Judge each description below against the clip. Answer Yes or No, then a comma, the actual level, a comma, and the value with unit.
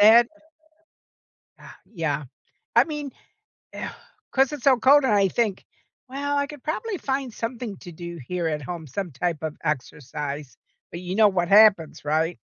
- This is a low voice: No, high, 195 Hz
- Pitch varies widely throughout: Yes, wide, 8.3 semitones